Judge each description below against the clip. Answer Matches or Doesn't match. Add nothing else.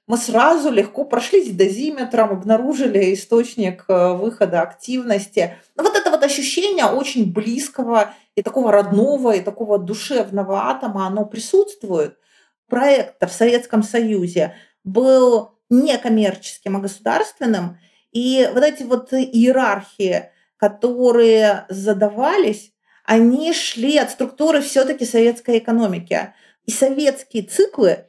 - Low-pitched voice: Doesn't match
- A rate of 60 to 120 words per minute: Matches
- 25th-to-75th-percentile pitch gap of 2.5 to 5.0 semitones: Matches